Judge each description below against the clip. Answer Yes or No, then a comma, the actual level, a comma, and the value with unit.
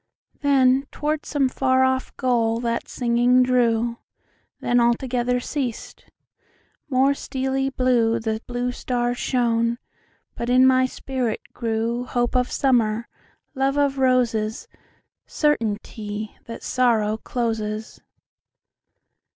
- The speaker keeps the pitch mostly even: Yes, narrow, 2.1 semitones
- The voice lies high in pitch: Yes, high, 245 Hz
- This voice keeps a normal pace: No, slow, 95 wpm